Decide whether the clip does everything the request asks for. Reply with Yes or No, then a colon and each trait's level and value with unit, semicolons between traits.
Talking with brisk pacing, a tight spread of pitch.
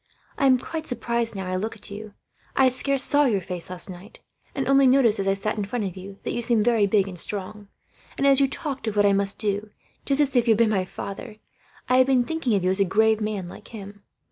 No: fast, 260 wpm; average, 4.4 semitones